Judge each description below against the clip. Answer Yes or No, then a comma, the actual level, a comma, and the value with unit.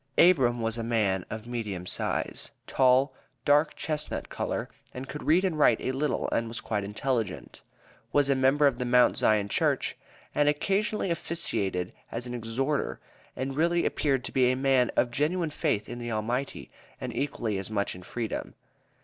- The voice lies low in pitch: Yes, low, 125 Hz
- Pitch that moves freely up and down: No, average, 4.5 semitones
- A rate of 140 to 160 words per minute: No, average, 175 wpm